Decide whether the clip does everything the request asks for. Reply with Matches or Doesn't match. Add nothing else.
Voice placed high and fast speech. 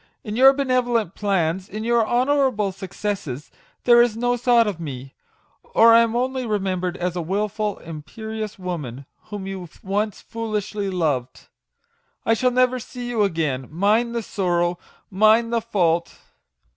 Doesn't match